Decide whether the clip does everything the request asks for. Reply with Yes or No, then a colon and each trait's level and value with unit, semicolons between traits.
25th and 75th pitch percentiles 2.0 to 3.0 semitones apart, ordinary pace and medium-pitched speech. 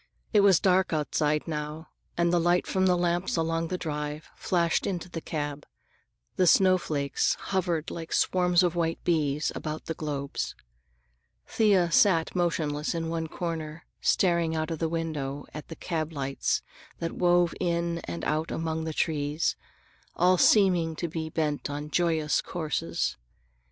Yes: narrow, 2.4 semitones; average, 150 wpm; medium, 165 Hz